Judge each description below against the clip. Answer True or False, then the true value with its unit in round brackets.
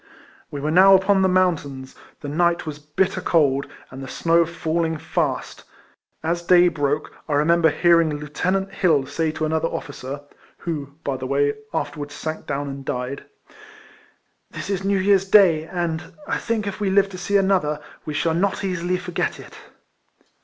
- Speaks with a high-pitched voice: False (165 Hz)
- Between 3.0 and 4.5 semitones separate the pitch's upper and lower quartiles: True (4.0 semitones)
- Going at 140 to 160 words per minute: False (170 wpm)